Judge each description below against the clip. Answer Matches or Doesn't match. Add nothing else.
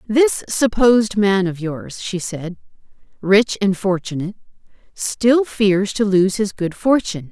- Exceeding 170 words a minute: Doesn't match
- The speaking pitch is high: Matches